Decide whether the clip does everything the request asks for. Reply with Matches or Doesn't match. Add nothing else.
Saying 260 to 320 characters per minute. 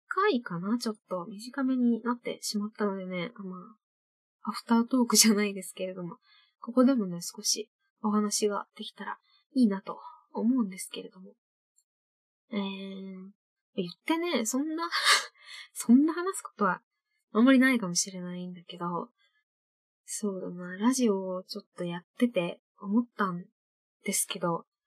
Matches